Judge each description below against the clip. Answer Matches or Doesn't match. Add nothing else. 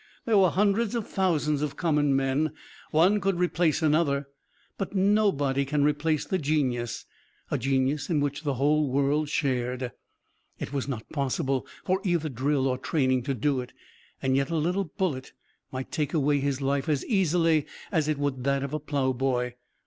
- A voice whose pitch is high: Doesn't match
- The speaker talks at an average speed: Matches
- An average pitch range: Matches